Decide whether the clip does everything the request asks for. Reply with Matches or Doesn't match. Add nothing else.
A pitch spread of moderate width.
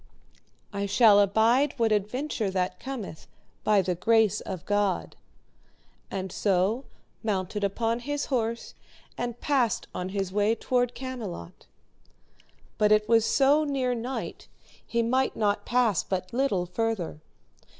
Matches